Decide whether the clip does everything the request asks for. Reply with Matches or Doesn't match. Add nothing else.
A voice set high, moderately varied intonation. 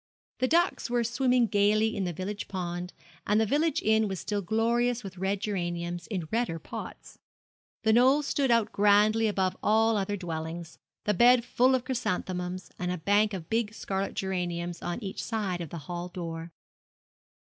Matches